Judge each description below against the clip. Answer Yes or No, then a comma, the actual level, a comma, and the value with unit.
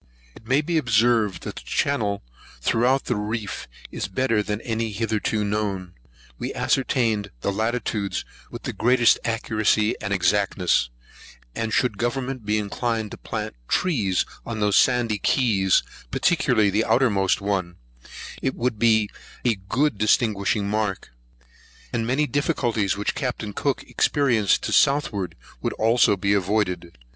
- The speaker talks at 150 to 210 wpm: No, average, 140 wpm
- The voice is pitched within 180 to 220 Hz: No, low, 110 Hz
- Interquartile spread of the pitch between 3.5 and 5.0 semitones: No, average, 3.1 semitones